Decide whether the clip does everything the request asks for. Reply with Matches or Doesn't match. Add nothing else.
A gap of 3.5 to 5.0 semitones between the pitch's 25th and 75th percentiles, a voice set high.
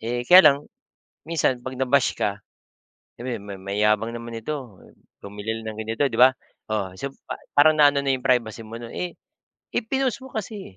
Doesn't match